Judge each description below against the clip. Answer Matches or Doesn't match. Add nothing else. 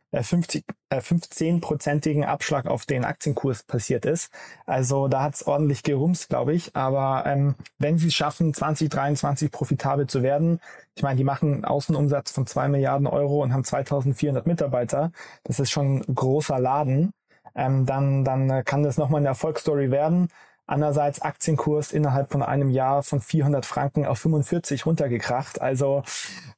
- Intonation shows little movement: Matches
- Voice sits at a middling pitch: Matches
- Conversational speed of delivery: Matches